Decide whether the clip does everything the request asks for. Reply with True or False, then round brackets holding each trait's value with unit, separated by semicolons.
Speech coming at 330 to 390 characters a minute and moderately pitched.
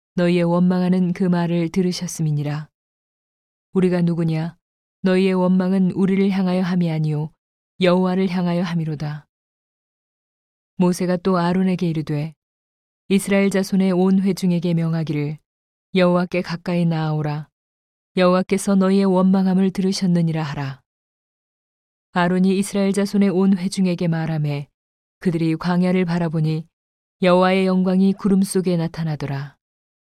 False (305 characters per minute; 180 Hz)